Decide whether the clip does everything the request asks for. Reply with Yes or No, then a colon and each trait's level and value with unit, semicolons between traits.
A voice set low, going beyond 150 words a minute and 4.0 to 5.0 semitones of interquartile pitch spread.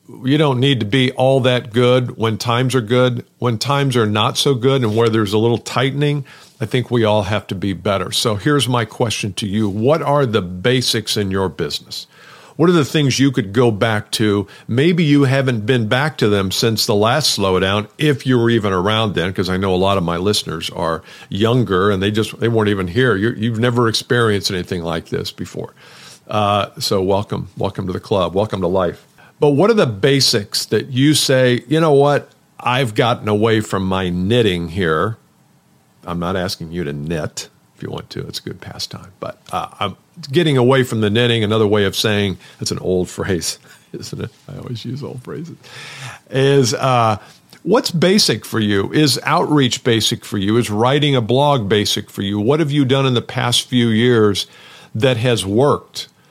Yes: low, 115 Hz; fast, 205 wpm; average, 4.4 semitones